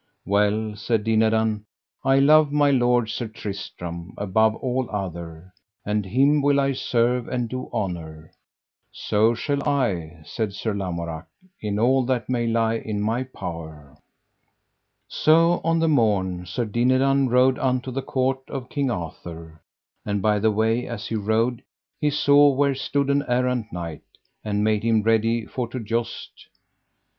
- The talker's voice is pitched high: No, low, 115 Hz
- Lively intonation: No, average, 4.2 semitones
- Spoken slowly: No, average, 150 wpm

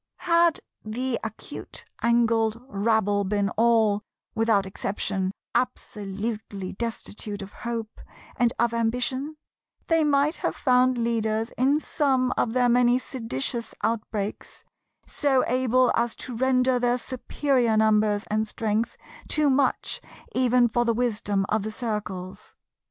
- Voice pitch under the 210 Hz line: No, high, 230 Hz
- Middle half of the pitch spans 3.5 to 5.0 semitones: No, average, 2.9 semitones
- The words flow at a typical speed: No, slow, 125 wpm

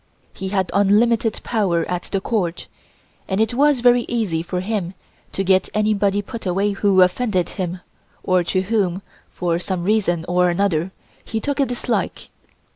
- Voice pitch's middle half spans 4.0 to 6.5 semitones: No, average, 3.4 semitones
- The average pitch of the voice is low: No, high, 195 Hz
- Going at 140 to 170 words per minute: Yes, average, 160 wpm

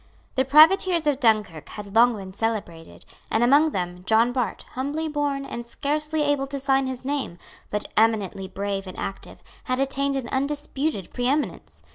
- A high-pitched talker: Yes, very high, 260 Hz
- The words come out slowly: No, average, 160 wpm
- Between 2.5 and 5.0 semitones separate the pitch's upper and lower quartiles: No, wide, 5.5 semitones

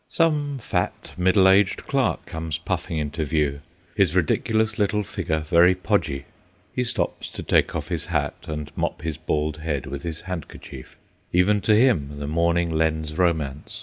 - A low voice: Yes, very low, 85 Hz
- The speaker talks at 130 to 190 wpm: Yes, average, 160 wpm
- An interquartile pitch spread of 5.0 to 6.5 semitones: No, average, 3.7 semitones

